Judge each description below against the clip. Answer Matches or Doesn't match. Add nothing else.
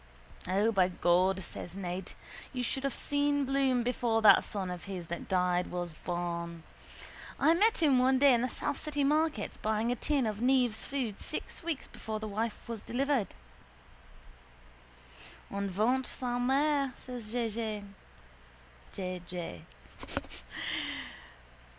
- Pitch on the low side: Doesn't match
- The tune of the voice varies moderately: Doesn't match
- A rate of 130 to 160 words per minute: Matches